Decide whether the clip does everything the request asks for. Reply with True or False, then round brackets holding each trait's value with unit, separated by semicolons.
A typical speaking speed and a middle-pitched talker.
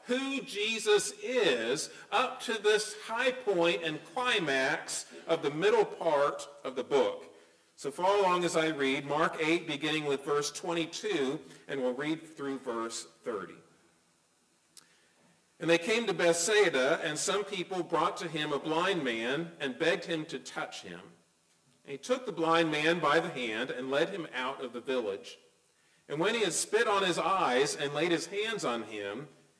True (170 wpm; 160 Hz)